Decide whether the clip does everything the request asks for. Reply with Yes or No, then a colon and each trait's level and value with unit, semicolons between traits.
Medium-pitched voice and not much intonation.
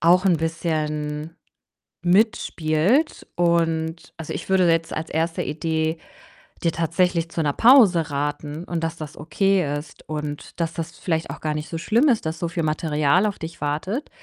Yes: medium, 165 Hz; narrow, 2.3 semitones